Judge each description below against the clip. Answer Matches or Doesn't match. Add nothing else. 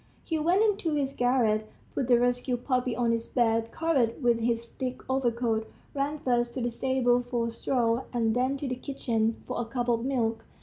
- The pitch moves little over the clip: Matches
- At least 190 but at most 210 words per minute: Matches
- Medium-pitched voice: Doesn't match